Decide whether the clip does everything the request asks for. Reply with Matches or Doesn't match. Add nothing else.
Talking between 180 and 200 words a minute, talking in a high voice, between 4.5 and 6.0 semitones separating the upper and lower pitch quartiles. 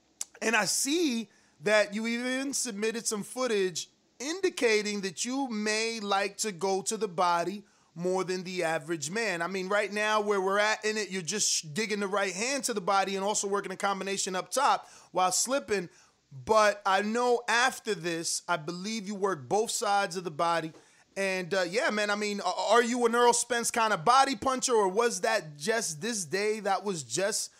Doesn't match